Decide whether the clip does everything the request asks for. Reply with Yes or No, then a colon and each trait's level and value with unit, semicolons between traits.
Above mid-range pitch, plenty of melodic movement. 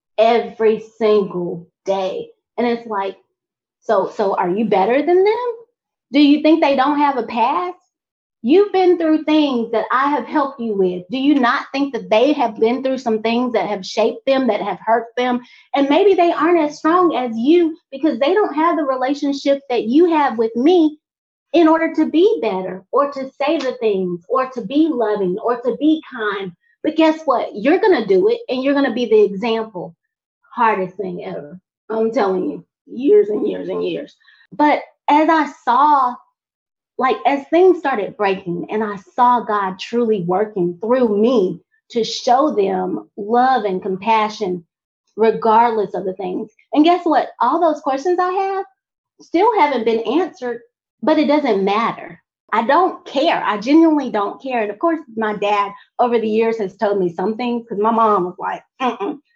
Yes: high, 245 Hz; wide, 6.3 semitones